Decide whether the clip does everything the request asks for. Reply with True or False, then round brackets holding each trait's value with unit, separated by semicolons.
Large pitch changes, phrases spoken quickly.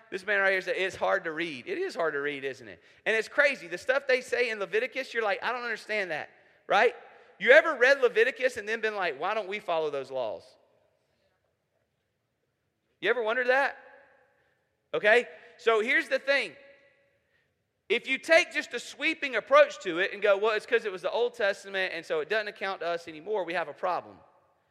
True (6.2 semitones; 210 wpm)